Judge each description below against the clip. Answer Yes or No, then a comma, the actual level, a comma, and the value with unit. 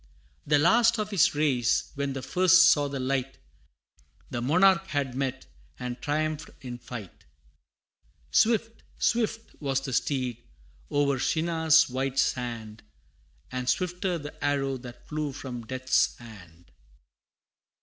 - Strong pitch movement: No, average, 4.4 semitones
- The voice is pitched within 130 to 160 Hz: Yes, medium, 140 Hz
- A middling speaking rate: No, slow, 125 wpm